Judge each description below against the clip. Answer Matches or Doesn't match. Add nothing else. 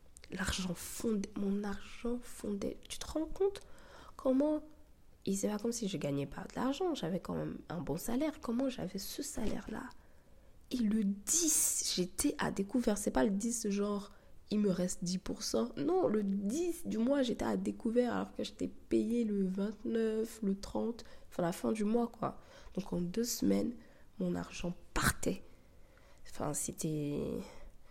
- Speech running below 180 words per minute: Matches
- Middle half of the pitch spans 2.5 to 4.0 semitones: Doesn't match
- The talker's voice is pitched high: Matches